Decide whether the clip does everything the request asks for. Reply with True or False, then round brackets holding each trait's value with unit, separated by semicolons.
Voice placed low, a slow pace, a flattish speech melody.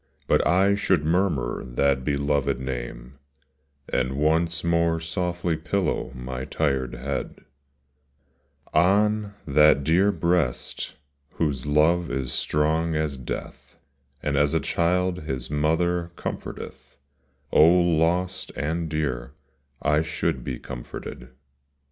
False (75 Hz; 110 wpm; 4.1 semitones)